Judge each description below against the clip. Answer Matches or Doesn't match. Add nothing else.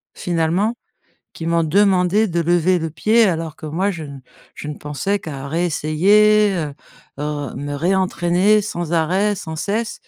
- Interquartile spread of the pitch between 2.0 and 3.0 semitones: Doesn't match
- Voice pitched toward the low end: Doesn't match